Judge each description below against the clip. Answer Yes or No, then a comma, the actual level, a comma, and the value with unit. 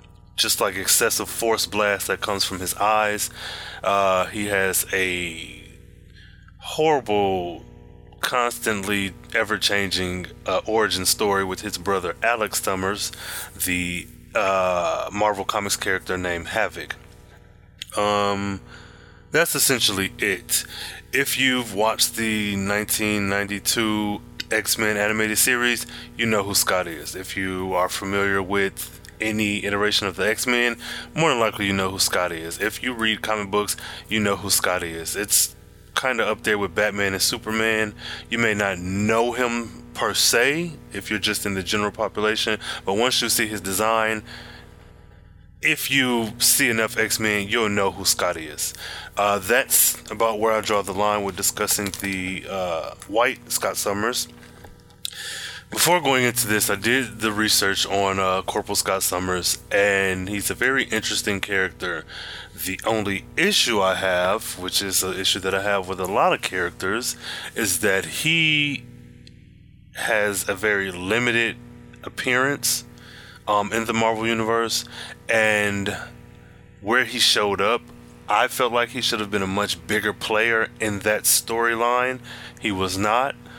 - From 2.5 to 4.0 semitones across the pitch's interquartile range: Yes, average, 2.8 semitones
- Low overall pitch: Yes, low, 105 Hz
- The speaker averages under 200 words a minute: Yes, average, 150 wpm